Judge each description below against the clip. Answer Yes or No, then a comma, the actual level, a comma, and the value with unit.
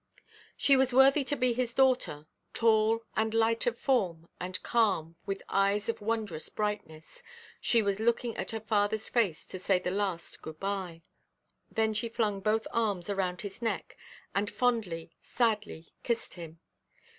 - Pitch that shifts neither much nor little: Yes, average, 3.7 semitones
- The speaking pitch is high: Yes, high, 215 Hz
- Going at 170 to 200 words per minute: No, average, 155 wpm